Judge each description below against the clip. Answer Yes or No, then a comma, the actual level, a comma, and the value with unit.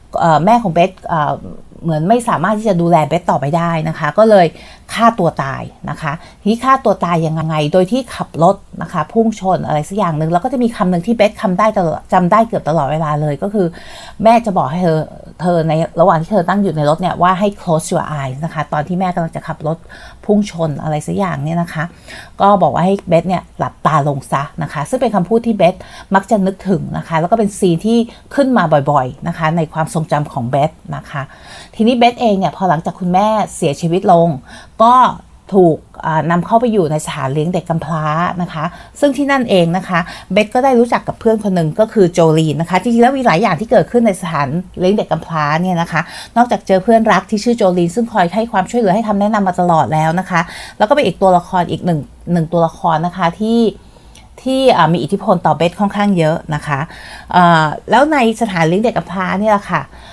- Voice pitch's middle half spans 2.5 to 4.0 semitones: No, average, 4.6 semitones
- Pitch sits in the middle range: Yes, medium, 180 Hz